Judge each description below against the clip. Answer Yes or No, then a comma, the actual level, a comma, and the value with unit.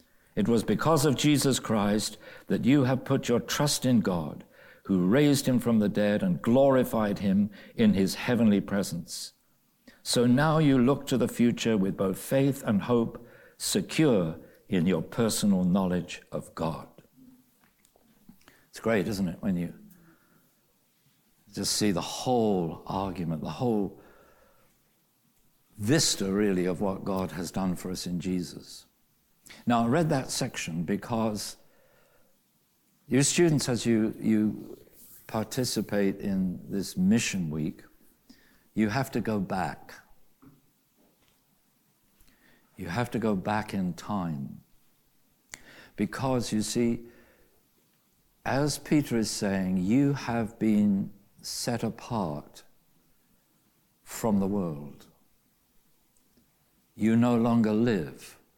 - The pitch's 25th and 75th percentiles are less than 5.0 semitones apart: No, wide, 5.4 semitones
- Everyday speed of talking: No, slow, 120 wpm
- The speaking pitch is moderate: No, low, 115 Hz